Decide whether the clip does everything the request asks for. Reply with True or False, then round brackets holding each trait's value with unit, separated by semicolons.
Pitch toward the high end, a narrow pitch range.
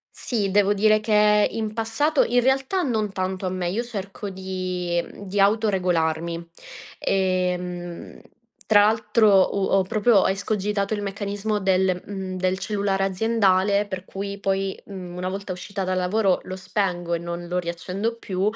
True (195 Hz; 2.3 semitones)